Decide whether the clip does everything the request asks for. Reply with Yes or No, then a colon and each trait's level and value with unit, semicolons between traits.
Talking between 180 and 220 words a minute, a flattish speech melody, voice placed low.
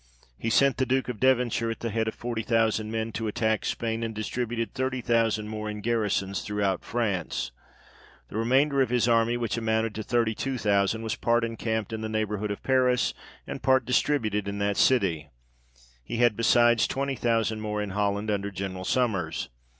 Yes: average, 185 wpm; narrow, 2.3 semitones; low, 110 Hz